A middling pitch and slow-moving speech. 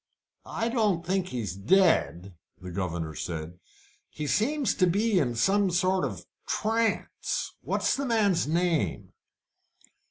Yes: medium, 180 Hz; slow, 125 wpm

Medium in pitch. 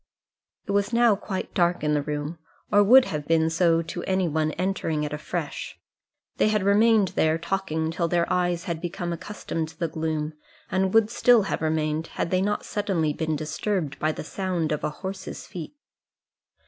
Yes: medium, 170 Hz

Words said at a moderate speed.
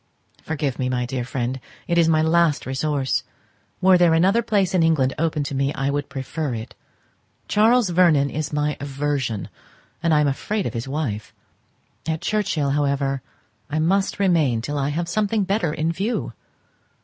Yes: average, 170 wpm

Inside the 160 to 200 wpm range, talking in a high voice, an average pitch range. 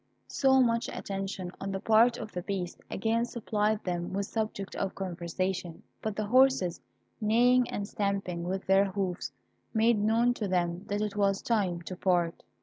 Yes: average, 165 wpm; high, 200 Hz; average, 3.2 semitones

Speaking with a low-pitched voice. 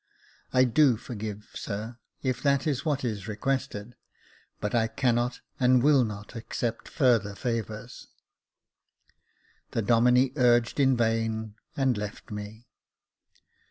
Yes: low, 120 Hz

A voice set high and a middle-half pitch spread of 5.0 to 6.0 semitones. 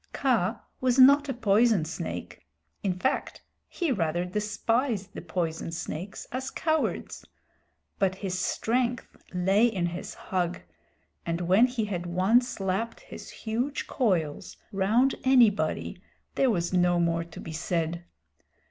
Yes: high, 195 Hz; wide, 5.6 semitones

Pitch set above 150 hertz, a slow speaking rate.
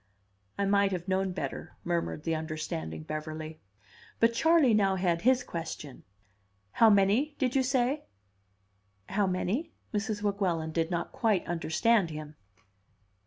Yes: high, 190 Hz; slow, 130 wpm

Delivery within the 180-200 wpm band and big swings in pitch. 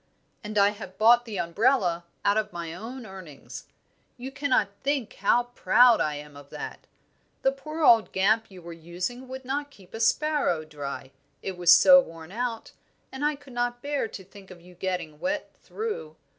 Yes: average, 185 wpm; wide, 6.8 semitones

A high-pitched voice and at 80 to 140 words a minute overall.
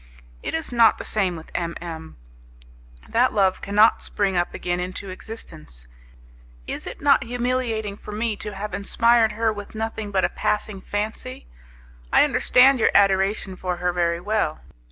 No: high, 205 Hz; average, 160 wpm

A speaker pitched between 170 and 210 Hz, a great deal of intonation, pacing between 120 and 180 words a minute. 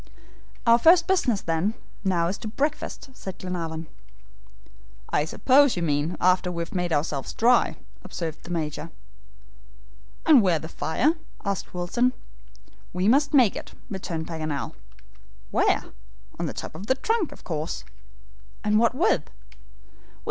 Yes: medium, 185 Hz; wide, 7.3 semitones; average, 140 wpm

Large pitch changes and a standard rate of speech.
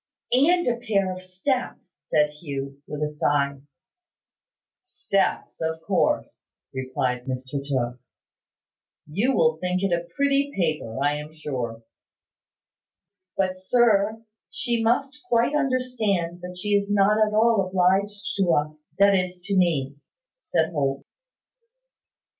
No: wide, 6.8 semitones; slow, 125 wpm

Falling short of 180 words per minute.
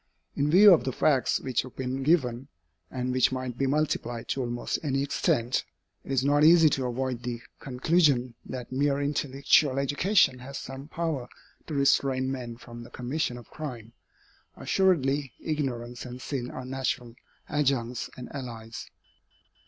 Yes: average, 150 wpm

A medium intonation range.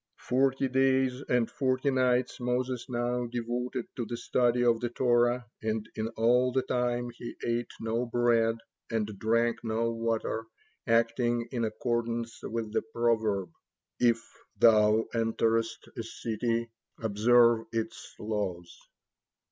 No: narrow, 1.5 semitones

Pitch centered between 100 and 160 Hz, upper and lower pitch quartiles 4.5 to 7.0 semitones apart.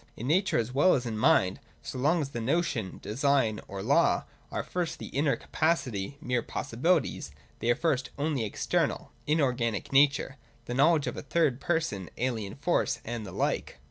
Yes: low, 135 Hz; average, 5.1 semitones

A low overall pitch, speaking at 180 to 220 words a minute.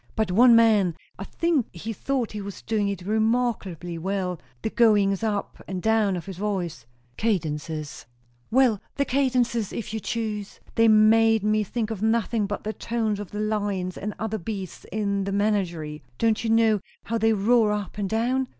No: high, 210 Hz; average, 185 wpm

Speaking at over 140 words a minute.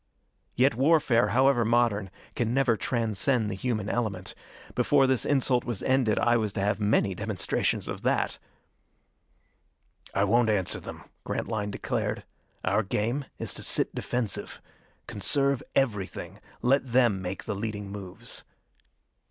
No: slow, 135 wpm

